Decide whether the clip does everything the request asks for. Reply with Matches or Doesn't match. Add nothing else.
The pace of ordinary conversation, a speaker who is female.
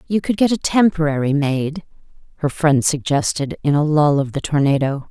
Matches